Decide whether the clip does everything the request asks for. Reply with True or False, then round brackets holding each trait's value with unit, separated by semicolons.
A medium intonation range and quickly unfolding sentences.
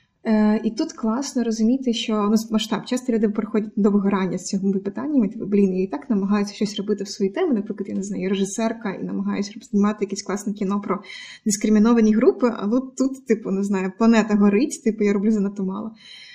False (2.1 semitones; 190 wpm)